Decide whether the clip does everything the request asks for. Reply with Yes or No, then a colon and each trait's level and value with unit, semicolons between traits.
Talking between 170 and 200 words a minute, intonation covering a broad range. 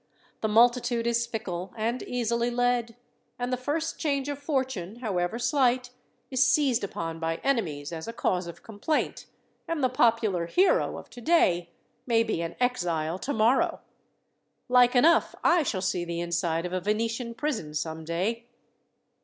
No: average, 155 wpm; wide, 6.0 semitones